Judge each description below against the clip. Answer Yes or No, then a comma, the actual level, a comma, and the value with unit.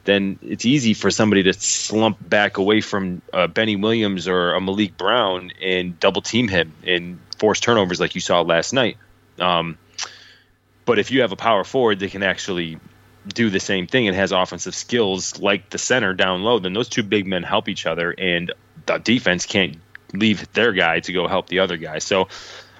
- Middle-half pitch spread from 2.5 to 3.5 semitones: Yes, average, 2.8 semitones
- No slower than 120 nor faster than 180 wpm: No, average, 195 wpm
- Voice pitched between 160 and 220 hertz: No, very low, 95 Hz